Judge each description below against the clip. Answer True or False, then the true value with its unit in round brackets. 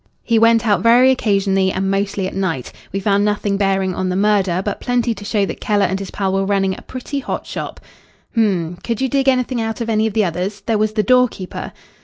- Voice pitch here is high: True (205 Hz)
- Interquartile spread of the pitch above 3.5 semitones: False (2.9 semitones)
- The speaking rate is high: True (235 wpm)